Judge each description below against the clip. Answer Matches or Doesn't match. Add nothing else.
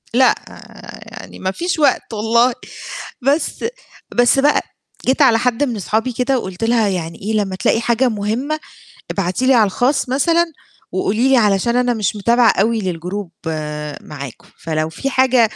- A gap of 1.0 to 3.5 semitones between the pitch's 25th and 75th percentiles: Doesn't match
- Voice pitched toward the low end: Doesn't match